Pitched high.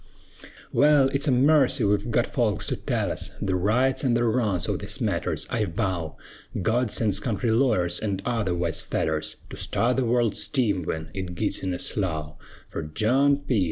No: low, 110 Hz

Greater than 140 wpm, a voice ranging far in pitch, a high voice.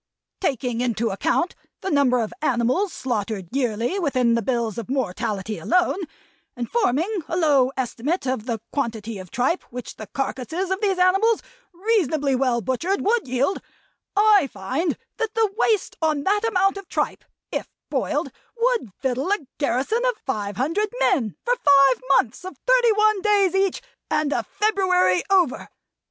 Yes: average, 155 wpm; wide, 8.2 semitones; very high, 285 Hz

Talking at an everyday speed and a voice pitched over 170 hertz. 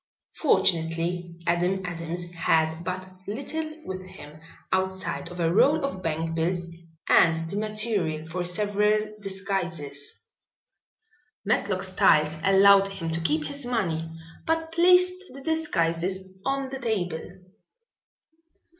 No: slow, 110 wpm; medium, 185 Hz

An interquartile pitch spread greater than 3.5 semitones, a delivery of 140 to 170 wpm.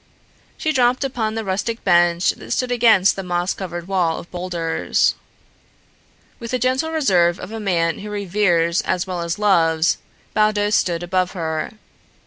Yes: average, 4.0 semitones; average, 155 wpm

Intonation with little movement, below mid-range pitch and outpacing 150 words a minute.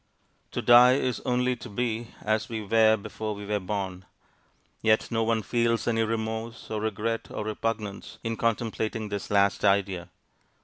Yes: narrow, 1.8 semitones; low, 110 Hz; average, 160 wpm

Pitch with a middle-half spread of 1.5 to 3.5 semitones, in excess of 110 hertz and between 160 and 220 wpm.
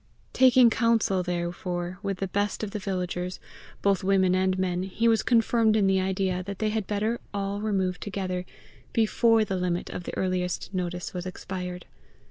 Yes: narrow, 2.6 semitones; high, 190 Hz; average, 170 wpm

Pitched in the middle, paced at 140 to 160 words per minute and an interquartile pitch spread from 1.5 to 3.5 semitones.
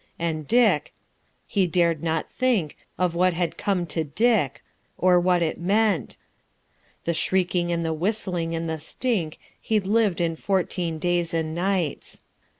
Yes: medium, 175 Hz; average, 150 wpm; average, 2.9 semitones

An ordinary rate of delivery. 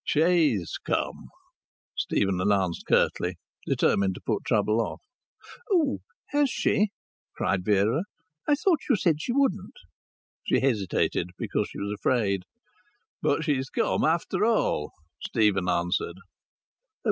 No: slow, 120 wpm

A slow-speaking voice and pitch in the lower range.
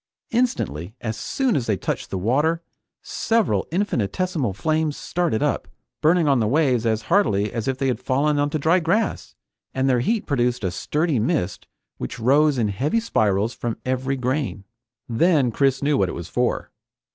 No: average, 170 wpm; low, 130 Hz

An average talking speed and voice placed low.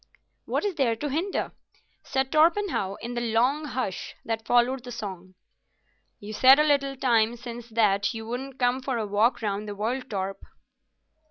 No: average, 170 wpm; high, 240 Hz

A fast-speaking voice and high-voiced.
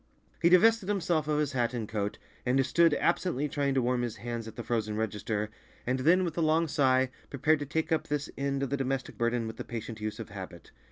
No: fast, 230 wpm; low, 135 Hz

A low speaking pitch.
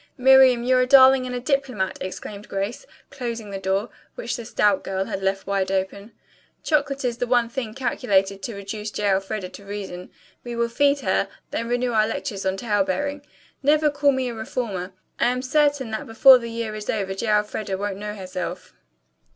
No: high, 225 Hz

